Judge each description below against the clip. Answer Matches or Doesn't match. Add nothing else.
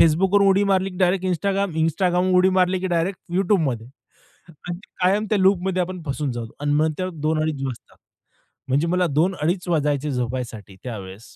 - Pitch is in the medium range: Matches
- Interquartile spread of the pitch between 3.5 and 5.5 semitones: Matches